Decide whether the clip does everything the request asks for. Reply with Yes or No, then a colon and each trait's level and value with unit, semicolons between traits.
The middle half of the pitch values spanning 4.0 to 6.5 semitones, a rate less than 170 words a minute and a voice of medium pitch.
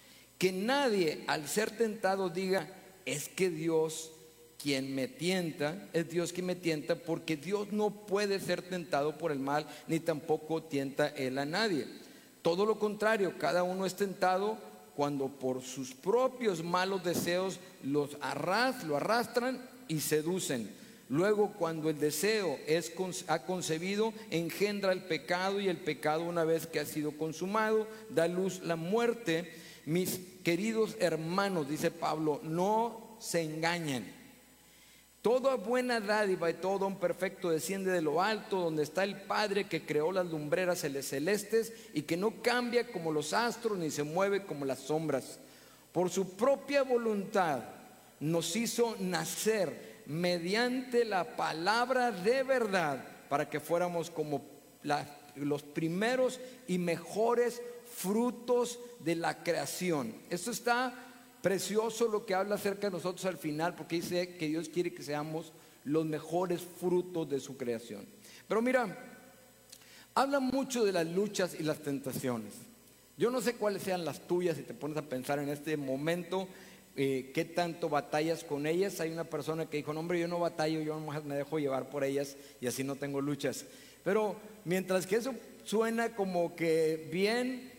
Yes: average, 5.3 semitones; average, 150 wpm; medium, 175 Hz